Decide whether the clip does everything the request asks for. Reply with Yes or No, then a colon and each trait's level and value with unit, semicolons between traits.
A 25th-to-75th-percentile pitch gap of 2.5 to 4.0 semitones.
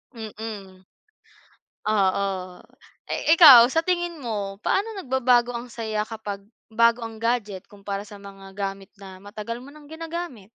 No: average, 4.7 semitones